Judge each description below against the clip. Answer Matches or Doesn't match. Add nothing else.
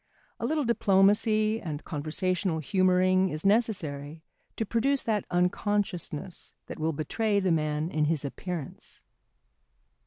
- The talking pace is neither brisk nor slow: Doesn't match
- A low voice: Doesn't match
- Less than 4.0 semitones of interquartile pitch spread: Doesn't match